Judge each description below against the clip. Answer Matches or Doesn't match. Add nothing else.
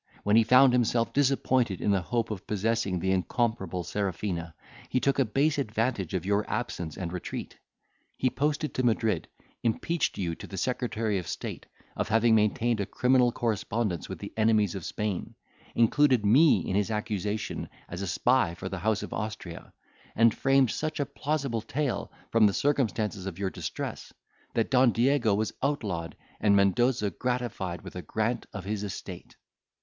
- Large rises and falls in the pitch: Doesn't match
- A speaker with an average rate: Matches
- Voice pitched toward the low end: Matches